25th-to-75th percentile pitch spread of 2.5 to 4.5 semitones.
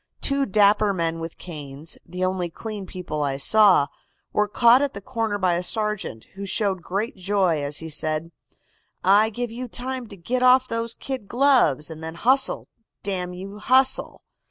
No: average, 5.3 semitones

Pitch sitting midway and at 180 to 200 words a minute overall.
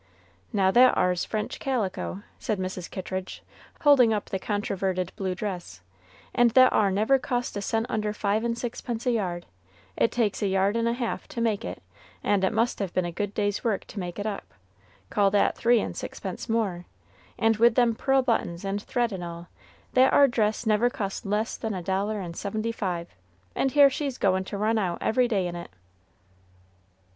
No: high, 210 Hz; average, 195 wpm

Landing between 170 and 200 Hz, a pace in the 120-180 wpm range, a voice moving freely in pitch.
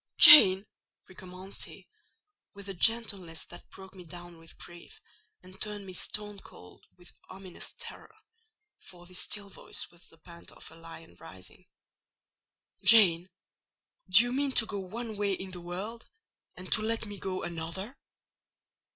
No: high, 190 Hz; average, 145 wpm; average, 3.4 semitones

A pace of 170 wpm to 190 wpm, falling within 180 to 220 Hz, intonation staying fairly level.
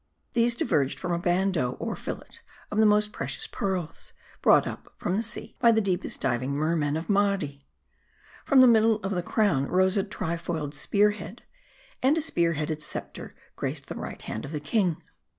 No: average, 185 wpm; medium, 185 Hz; wide, 5.5 semitones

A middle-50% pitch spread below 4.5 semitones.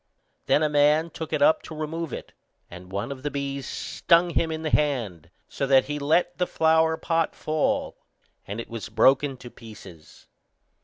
No: average, 4.8 semitones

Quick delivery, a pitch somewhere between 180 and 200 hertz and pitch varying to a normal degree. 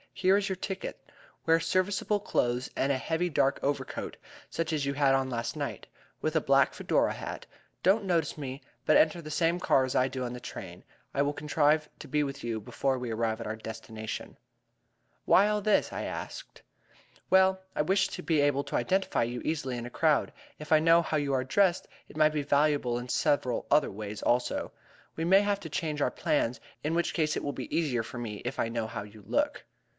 No: fast, 215 wpm; medium, 145 Hz; average, 4.9 semitones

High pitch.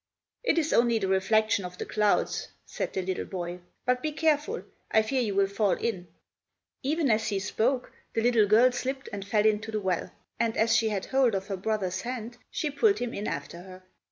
Yes: high, 220 Hz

